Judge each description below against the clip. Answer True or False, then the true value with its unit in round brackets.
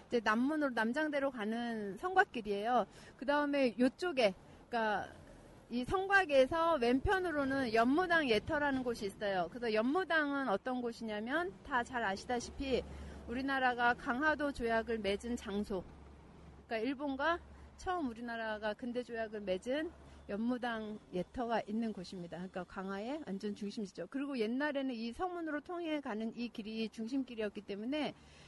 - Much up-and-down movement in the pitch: False (4.8 semitones)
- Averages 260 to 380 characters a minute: True (335 characters per minute)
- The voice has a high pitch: True (240 Hz)